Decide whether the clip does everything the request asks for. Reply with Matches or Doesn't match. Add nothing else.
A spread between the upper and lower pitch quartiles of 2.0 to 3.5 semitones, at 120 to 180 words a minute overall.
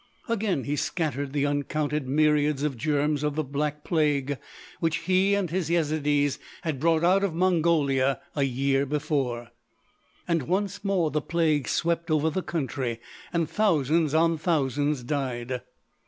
Matches